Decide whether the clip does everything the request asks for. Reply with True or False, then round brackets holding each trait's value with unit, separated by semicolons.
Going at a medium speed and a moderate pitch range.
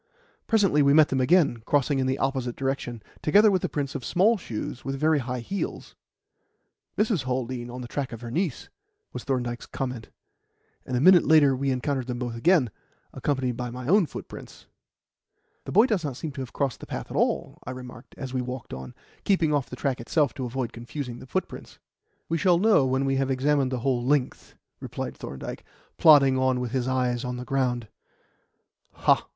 True (190 wpm; 3.0 semitones)